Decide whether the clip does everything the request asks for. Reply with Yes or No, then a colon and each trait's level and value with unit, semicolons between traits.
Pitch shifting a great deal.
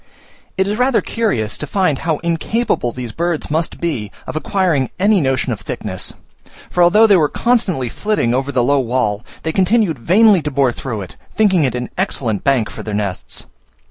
Yes: wide, 7.5 semitones